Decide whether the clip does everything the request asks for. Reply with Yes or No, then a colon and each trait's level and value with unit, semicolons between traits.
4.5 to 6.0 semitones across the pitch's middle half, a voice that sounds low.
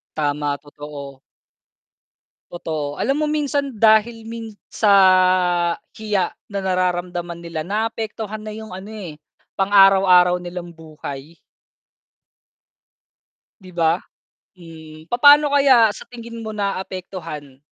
No: average, 5.1 semitones; medium, 185 Hz